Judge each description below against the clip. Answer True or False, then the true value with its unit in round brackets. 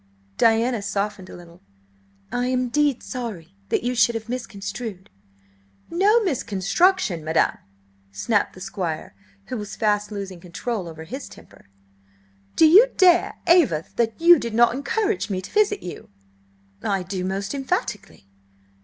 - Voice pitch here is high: True (225 Hz)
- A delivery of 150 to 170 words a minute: False (140 wpm)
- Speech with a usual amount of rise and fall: False (6.4 semitones)